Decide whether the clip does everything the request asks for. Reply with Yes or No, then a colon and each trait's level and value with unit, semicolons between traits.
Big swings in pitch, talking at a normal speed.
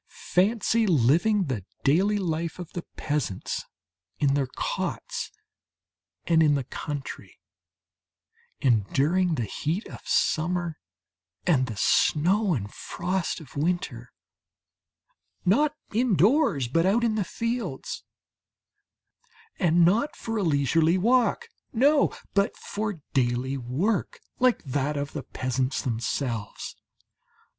No: wide, 6.9 semitones; slow, 110 wpm